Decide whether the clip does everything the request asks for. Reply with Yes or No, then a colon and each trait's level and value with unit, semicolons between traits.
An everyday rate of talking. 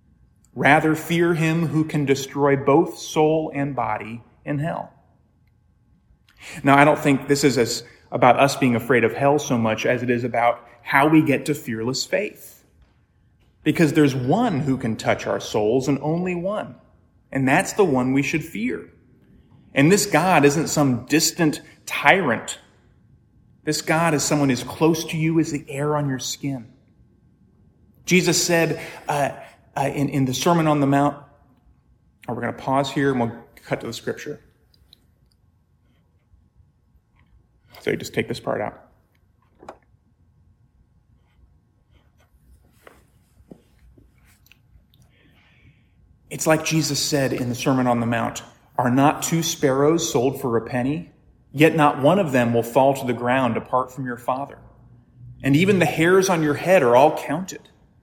Yes: average, 155 wpm